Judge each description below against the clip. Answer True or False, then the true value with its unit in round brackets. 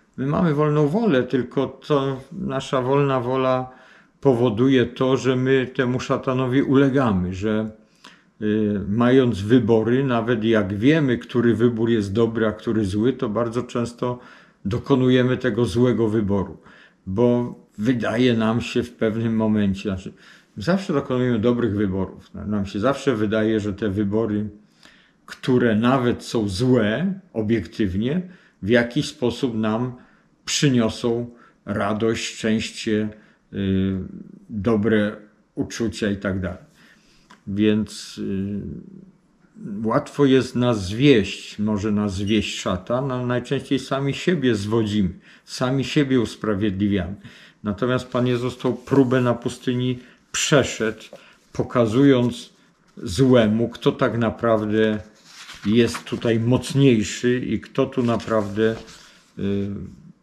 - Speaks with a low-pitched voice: True (120 Hz)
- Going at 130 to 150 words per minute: False (115 wpm)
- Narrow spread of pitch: False (3.3 semitones)